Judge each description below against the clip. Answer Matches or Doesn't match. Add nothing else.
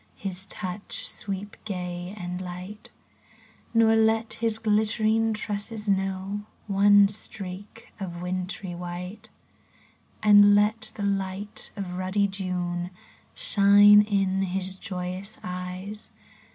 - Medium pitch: Doesn't match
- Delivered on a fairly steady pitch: Matches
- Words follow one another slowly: Matches